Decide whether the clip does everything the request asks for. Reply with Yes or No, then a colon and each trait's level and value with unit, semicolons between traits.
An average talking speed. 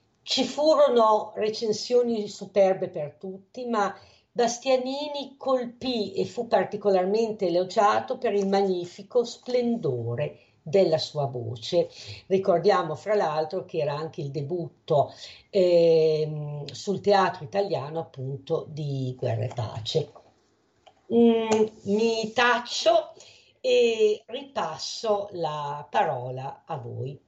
No: slow, 100 wpm